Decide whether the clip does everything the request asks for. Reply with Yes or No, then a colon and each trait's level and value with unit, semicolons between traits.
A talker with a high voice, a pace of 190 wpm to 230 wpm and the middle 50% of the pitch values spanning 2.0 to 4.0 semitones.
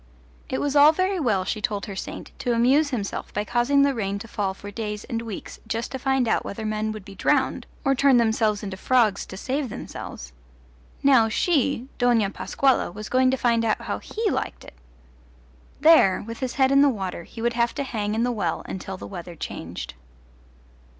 No: high, 230 Hz; fast, 205 wpm; average, 4.4 semitones